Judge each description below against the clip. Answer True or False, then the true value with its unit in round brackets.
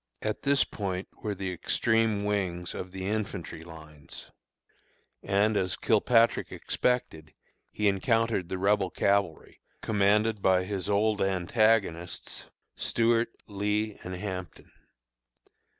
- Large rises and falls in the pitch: False (2.8 semitones)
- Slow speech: True (110 wpm)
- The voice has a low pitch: True (100 Hz)